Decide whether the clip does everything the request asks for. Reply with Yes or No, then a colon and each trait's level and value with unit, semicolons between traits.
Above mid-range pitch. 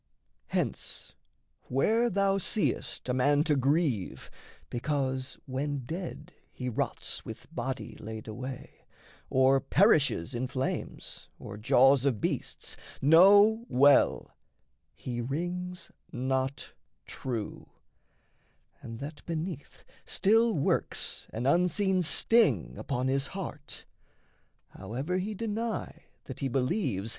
No: medium, 140 Hz